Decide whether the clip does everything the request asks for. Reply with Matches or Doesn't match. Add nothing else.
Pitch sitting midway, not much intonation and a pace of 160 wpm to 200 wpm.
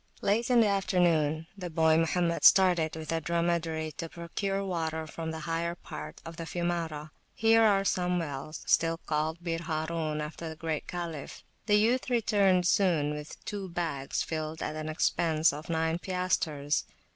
Matches